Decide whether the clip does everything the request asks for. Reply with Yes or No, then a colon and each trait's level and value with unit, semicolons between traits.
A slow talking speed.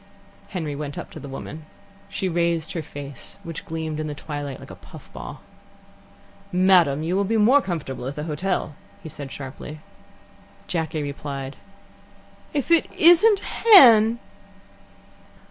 No: average, 145 wpm